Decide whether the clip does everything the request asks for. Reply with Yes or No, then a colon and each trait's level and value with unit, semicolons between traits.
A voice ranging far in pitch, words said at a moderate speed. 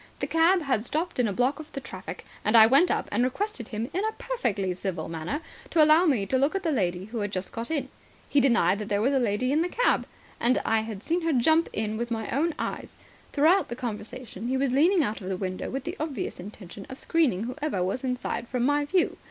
No: wide, 6.5 semitones; fast, 240 wpm